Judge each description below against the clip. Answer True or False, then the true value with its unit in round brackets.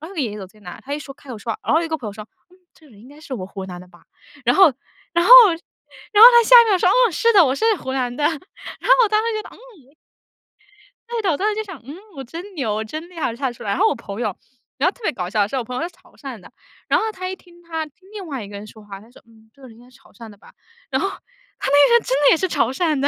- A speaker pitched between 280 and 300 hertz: True (285 Hz)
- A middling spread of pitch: False (8.6 semitones)